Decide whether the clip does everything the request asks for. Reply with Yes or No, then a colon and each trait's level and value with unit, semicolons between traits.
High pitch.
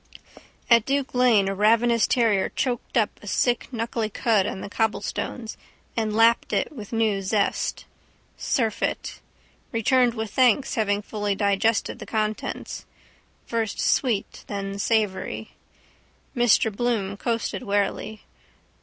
Yes: high, 220 Hz